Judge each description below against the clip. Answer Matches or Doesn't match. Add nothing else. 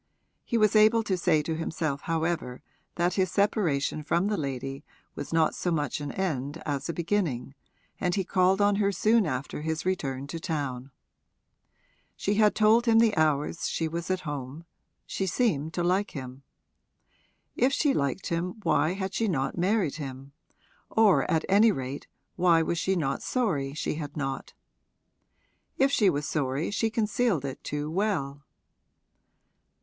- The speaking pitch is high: Doesn't match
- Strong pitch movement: Matches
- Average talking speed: Matches